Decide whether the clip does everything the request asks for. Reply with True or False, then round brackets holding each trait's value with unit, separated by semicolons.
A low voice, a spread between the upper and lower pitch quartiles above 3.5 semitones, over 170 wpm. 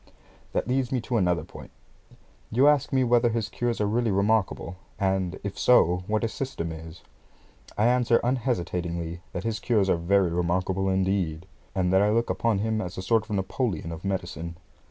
True (100 Hz; 4.7 semitones; 180 wpm)